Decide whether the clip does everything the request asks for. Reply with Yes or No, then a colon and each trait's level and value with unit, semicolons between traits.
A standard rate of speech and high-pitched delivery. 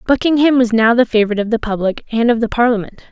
No: fast, 230 wpm; high, 230 Hz